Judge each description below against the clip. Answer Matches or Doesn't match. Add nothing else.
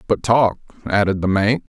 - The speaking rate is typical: Matches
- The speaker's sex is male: Matches